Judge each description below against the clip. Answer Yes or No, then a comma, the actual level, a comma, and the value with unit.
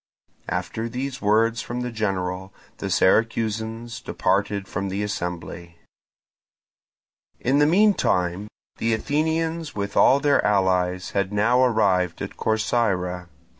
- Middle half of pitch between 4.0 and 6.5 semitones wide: Yes, average, 4.6 semitones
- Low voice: Yes, low, 110 Hz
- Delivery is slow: Yes, slow, 115 wpm